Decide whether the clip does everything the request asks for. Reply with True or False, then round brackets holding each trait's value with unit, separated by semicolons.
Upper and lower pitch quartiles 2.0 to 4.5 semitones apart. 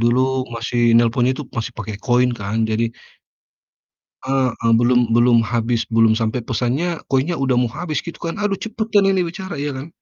False (4.9 semitones)